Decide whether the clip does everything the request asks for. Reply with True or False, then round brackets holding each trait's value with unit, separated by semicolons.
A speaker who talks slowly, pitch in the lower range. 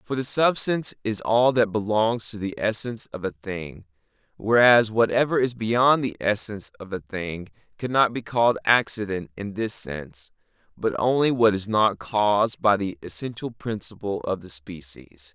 False (165 wpm; 105 Hz)